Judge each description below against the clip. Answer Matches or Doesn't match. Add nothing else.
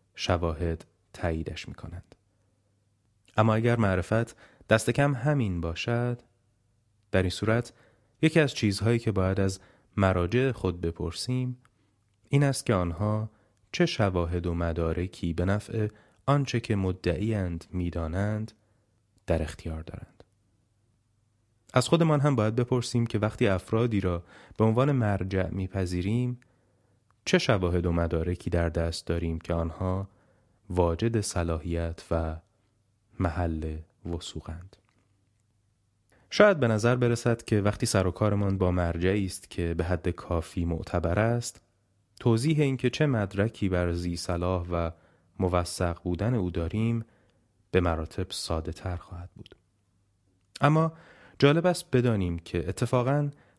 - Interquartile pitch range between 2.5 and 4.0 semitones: Doesn't match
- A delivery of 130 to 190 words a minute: Doesn't match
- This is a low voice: Matches